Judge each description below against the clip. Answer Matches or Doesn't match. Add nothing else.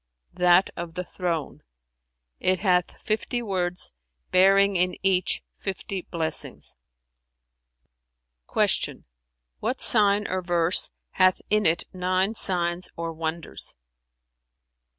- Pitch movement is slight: Matches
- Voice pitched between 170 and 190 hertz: Matches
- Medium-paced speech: Doesn't match